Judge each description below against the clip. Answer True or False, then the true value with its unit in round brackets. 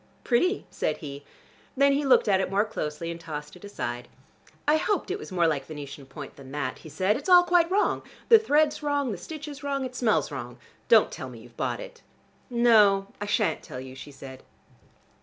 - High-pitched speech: True (200 Hz)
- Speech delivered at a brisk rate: True (210 wpm)